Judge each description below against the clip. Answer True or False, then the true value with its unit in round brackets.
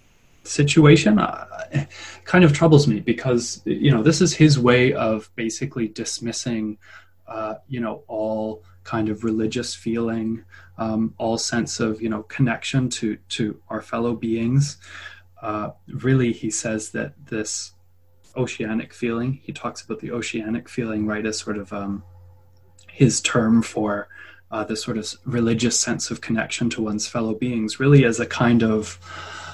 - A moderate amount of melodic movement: False (2.3 semitones)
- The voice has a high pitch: False (115 Hz)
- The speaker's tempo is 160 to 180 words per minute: False (150 wpm)